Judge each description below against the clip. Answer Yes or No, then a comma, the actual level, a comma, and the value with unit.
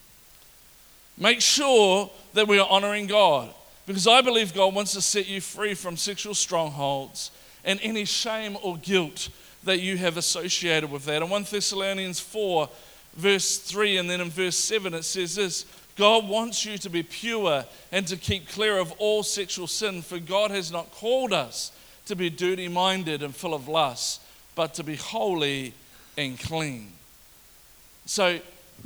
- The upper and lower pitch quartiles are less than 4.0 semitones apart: Yes, average, 3.1 semitones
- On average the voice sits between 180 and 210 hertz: Yes, high, 190 Hz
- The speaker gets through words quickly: No, average, 160 wpm